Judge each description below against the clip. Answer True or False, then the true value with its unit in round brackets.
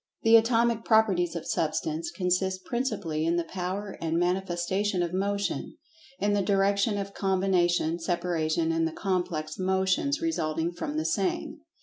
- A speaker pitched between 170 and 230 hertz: True (185 Hz)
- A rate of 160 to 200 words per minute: False (140 wpm)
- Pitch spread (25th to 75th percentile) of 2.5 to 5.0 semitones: True (3.3 semitones)